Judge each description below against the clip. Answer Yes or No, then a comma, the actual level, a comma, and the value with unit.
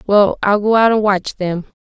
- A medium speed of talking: No, fast, 225 wpm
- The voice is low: No, high, 205 Hz